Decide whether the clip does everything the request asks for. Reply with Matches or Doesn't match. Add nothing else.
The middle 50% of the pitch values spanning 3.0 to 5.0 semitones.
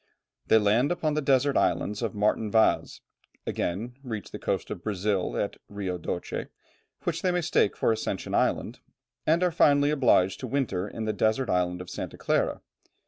Doesn't match